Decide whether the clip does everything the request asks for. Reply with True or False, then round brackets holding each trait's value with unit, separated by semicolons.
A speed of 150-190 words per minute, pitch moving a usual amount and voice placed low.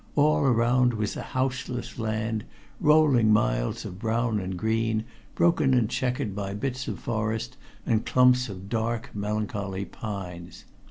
False (140 wpm; 3.4 semitones; 110 Hz)